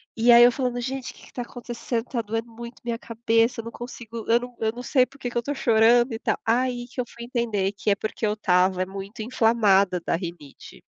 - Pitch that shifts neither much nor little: No, narrow, 2.0 semitones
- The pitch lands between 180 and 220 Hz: No, high, 230 Hz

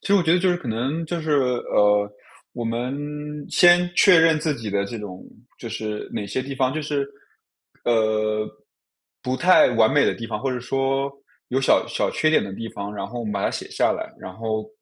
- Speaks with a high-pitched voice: No, low, 125 Hz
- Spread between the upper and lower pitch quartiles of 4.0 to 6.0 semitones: Yes, wide, 5.5 semitones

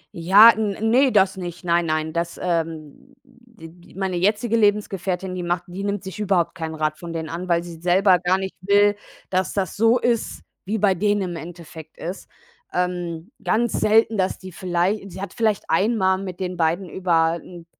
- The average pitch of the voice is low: No, medium, 185 Hz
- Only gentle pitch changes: No, average, 3.1 semitones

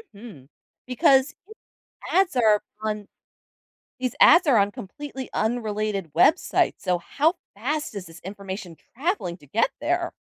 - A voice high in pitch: Yes, high, 220 Hz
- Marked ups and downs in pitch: Yes, wide, 6.9 semitones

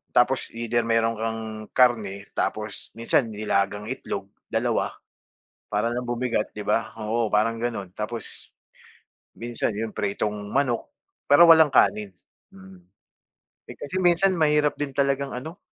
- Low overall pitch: Yes, low, 115 Hz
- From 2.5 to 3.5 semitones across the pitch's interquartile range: No, average, 4.2 semitones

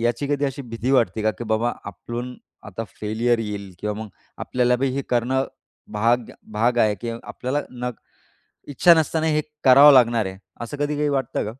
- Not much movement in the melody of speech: No, average, 3.5 semitones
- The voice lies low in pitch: Yes, low, 120 Hz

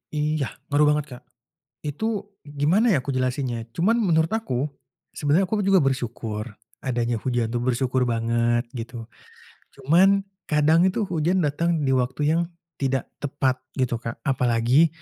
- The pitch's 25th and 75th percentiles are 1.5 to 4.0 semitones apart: No, average, 4.5 semitones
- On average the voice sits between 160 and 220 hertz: No, low, 135 Hz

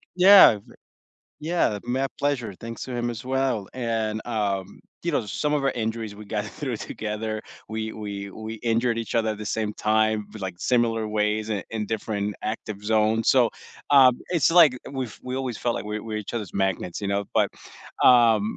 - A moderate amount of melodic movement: Yes, average, 3.0 semitones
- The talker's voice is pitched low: Yes, low, 110 Hz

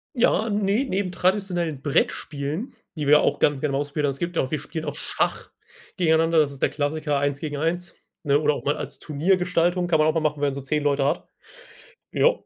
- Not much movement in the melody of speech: No, average, 3.4 semitones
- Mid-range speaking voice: Yes, medium, 155 Hz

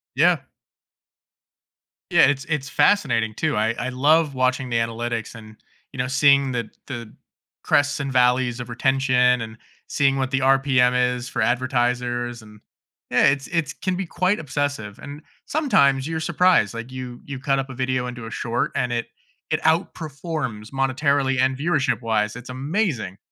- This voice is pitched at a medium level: No, low, 130 Hz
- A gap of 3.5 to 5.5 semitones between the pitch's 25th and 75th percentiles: No, average, 2.9 semitones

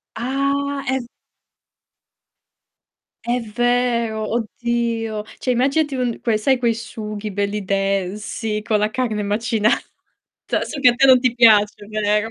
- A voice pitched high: Yes, high, 230 Hz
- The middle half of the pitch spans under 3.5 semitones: Yes, average, 2.8 semitones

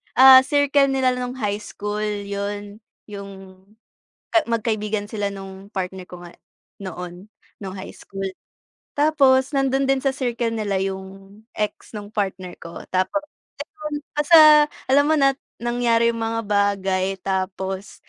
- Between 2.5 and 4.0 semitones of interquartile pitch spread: No, average, 5.1 semitones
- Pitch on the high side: Yes, high, 210 Hz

